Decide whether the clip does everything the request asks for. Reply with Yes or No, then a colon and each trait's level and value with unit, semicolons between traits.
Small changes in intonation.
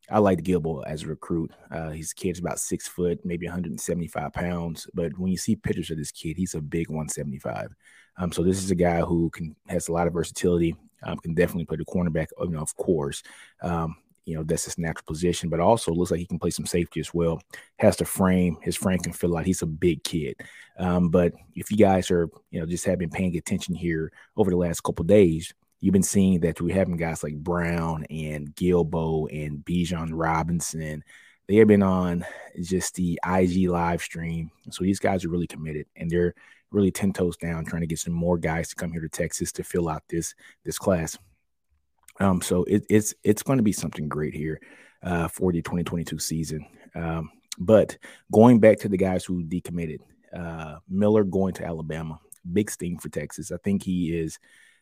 Yes: narrow, 1.9 semitones